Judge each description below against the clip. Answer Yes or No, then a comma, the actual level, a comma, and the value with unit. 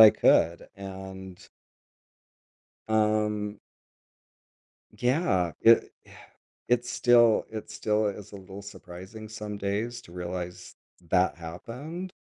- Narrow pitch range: No, average, 3.1 semitones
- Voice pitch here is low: Yes, low, 105 Hz